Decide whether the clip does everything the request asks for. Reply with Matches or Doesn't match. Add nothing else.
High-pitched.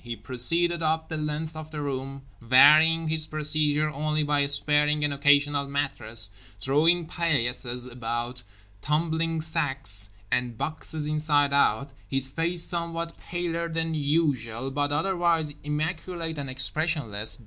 Doesn't match